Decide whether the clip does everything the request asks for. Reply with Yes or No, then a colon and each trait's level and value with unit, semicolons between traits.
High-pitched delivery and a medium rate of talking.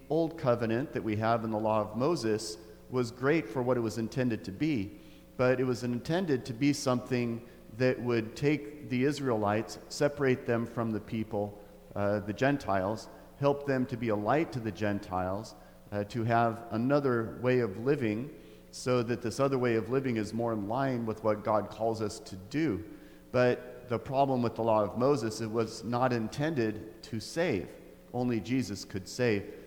No: low, 115 Hz; average, 185 wpm